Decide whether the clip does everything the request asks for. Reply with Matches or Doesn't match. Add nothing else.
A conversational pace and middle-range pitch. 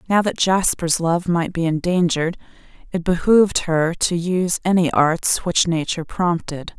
Matches